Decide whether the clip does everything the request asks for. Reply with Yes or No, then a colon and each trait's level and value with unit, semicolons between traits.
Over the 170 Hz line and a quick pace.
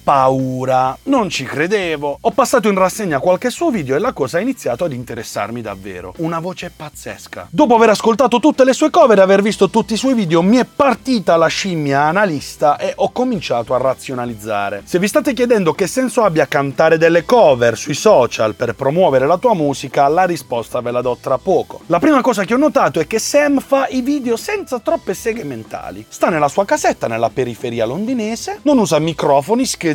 Yes: medium, 185 Hz; fast, 195 wpm